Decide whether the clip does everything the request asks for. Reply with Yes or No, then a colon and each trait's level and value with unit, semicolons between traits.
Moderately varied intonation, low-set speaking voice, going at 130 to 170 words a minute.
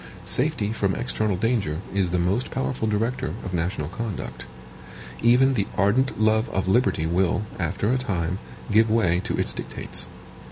Yes: average, 4.4 semitones; low, 105 Hz; average, 155 wpm